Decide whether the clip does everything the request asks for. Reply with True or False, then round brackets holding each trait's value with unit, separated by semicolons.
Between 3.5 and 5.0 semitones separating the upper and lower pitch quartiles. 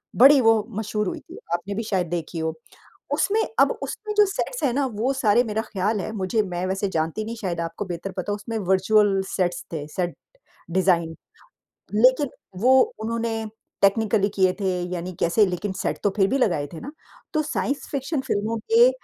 True (4.1 semitones)